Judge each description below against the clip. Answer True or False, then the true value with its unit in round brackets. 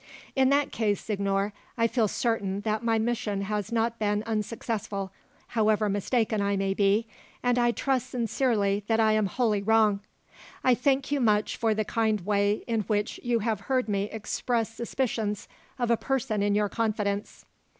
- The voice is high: True (220 Hz)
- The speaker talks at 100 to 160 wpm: False (170 wpm)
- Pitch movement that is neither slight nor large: False (2.3 semitones)